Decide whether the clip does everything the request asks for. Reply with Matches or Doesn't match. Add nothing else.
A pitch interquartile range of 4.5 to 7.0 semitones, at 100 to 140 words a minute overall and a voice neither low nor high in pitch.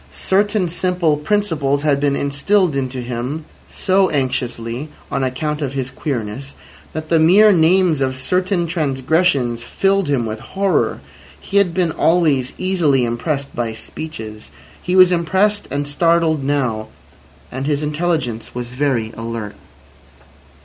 Matches